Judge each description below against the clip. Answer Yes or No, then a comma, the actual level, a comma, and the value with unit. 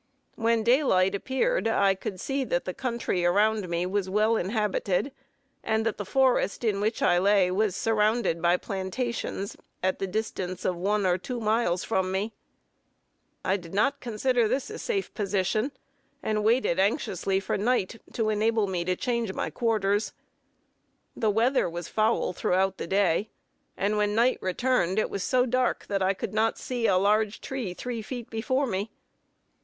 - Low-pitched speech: No, high, 210 Hz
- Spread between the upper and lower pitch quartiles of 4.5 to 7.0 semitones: No, average, 3.5 semitones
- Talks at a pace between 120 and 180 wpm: Yes, average, 170 wpm